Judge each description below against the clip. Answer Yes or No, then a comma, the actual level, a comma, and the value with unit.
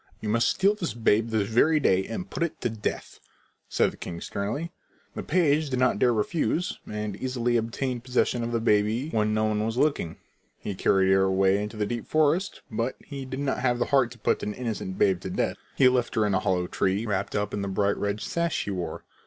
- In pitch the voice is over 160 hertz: No, low, 115 Hz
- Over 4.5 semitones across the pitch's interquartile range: No, average, 4.2 semitones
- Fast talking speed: Yes, fast, 225 wpm